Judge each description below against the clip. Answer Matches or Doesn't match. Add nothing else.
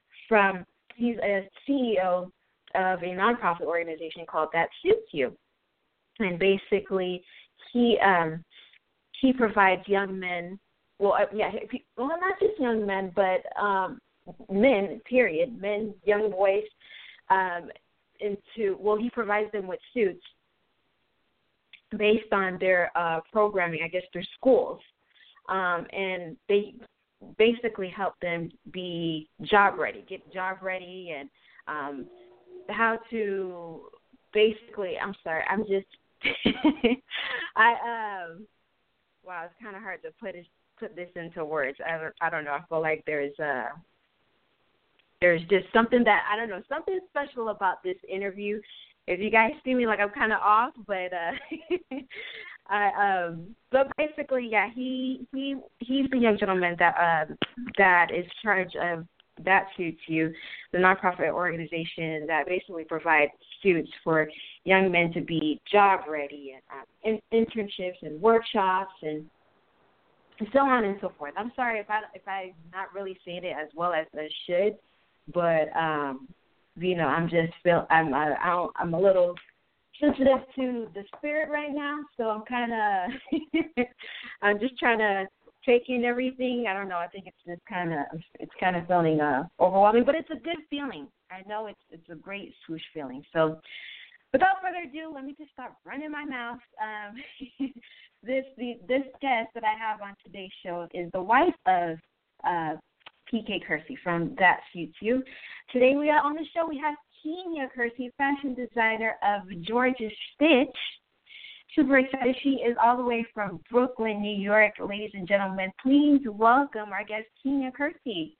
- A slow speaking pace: Doesn't match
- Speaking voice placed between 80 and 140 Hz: Doesn't match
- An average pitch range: Doesn't match